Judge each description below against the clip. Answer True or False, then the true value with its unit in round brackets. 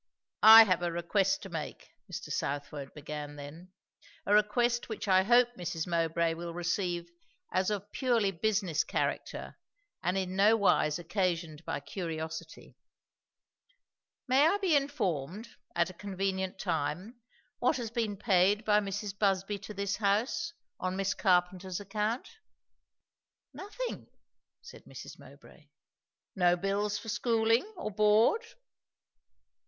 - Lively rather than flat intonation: False (3.9 semitones)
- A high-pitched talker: True (195 Hz)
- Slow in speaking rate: True (125 wpm)